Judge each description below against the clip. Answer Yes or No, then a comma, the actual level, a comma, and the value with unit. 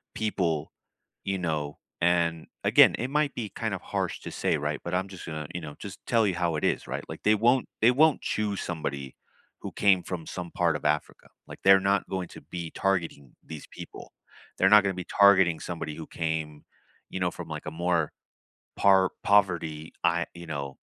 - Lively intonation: No, average, 3.6 semitones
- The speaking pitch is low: Yes, very low, 85 Hz